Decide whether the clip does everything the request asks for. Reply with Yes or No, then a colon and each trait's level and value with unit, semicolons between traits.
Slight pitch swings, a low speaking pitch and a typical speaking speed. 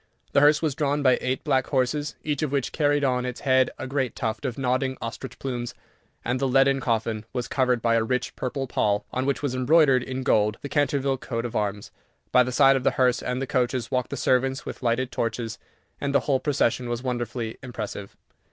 No: narrow, 2.1 semitones; low, 130 Hz; fast, 215 wpm